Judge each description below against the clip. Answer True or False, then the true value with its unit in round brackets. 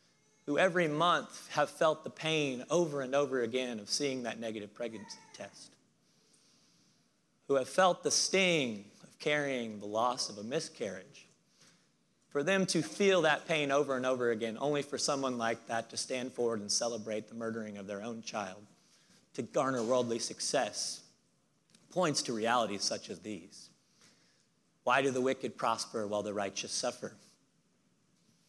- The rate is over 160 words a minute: False (155 wpm)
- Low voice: True (130 Hz)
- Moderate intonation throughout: True (4.5 semitones)